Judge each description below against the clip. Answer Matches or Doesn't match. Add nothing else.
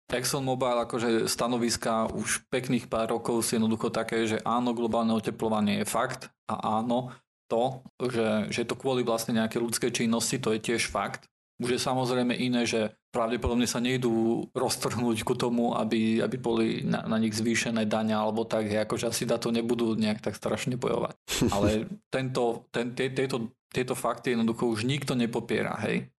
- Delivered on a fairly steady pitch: Matches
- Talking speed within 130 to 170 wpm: Matches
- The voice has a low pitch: Matches